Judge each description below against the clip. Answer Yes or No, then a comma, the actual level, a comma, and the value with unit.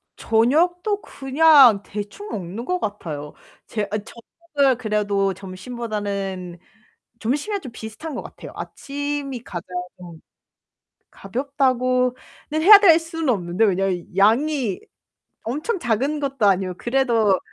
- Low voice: No, high, 240 Hz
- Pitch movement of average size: No, wide, 6.3 semitones